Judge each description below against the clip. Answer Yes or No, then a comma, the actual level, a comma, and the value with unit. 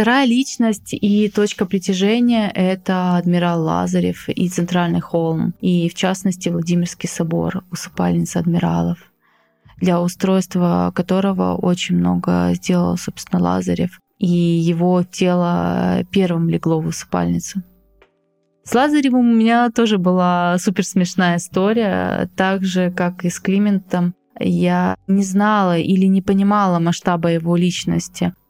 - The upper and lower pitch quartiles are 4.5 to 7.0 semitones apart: No, narrow, 2.6 semitones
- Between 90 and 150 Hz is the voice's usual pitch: No, medium, 180 Hz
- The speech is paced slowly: No, average, 120 wpm